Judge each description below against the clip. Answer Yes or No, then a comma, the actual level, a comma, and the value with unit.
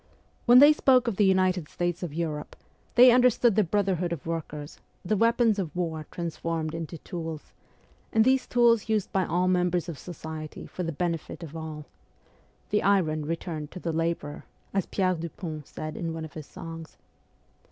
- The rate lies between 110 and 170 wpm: No, average, 180 wpm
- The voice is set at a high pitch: No, medium, 170 Hz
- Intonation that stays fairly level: No, average, 3.8 semitones